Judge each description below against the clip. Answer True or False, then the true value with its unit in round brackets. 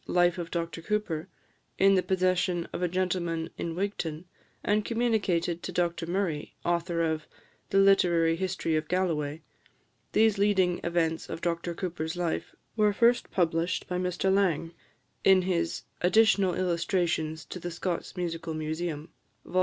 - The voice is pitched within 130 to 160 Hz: False (175 Hz)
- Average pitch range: False (2.2 semitones)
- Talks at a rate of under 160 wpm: True (145 wpm)